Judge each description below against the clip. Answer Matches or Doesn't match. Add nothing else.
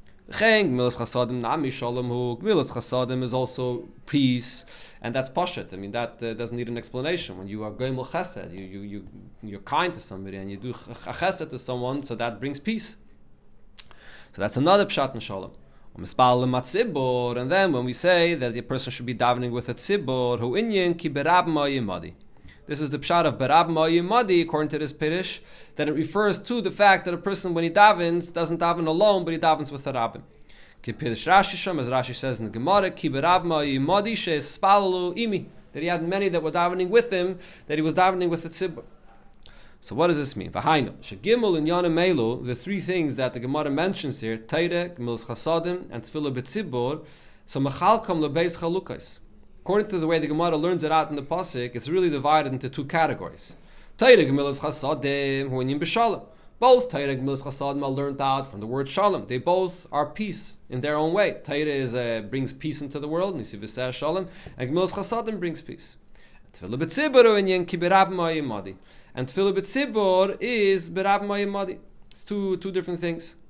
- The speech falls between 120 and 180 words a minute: Matches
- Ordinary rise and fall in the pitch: Doesn't match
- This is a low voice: Doesn't match